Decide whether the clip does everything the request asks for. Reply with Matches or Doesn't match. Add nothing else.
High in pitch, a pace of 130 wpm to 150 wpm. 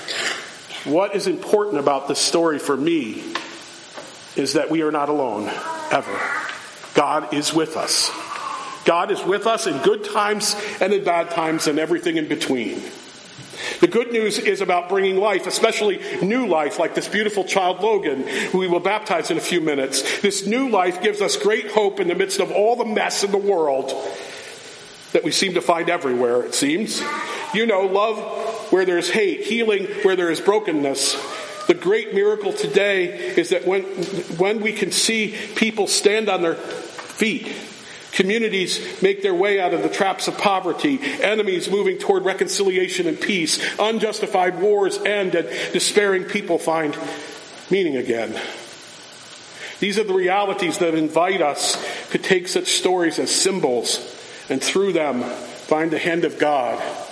Doesn't match